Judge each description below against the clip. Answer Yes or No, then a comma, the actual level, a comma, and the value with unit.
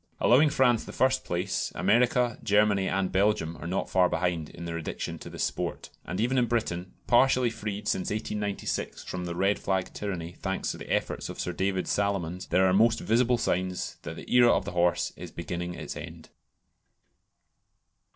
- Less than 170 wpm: No, average, 180 wpm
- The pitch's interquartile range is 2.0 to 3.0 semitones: No, average, 4.1 semitones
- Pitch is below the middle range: Yes, very low, 95 Hz